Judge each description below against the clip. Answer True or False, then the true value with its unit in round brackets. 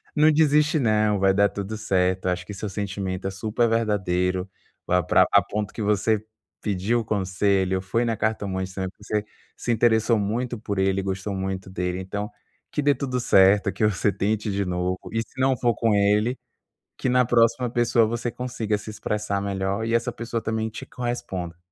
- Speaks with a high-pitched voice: False (105 Hz)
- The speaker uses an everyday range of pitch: True (3.3 semitones)